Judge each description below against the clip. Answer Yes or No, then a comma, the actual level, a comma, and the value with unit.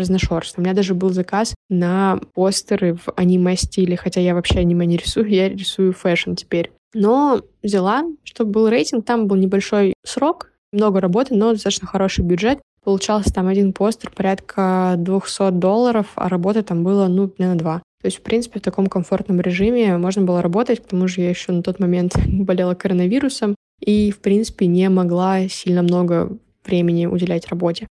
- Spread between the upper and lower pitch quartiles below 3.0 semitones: Yes, narrow, 2.4 semitones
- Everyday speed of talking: No, fast, 170 wpm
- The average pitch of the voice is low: No, high, 190 Hz